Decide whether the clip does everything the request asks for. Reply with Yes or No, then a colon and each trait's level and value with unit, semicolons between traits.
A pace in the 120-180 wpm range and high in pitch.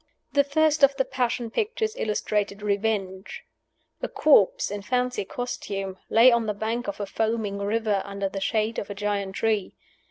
Yes: average, 165 wpm; high, 215 Hz